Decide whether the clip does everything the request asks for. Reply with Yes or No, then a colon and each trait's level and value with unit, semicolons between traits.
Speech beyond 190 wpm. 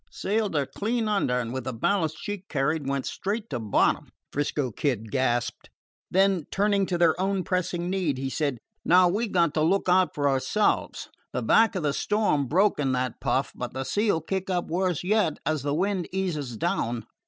Yes: average, 200 wpm